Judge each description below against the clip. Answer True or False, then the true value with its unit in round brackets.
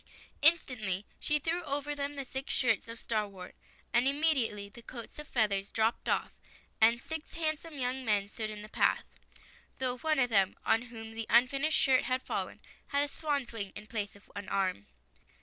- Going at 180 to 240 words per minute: True (185 wpm)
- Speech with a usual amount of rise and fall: True (4.9 semitones)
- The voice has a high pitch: True (240 Hz)